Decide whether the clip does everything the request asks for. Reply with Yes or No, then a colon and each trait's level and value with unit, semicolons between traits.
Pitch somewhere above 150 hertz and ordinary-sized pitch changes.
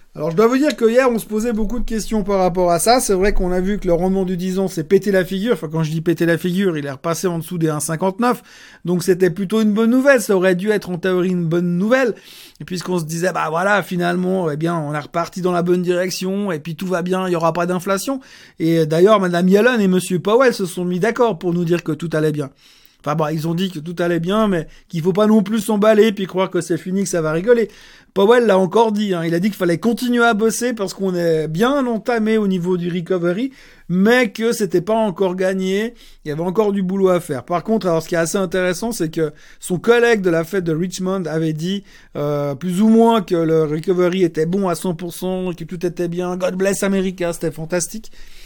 Yes: medium, 185 Hz; average, 3.7 semitones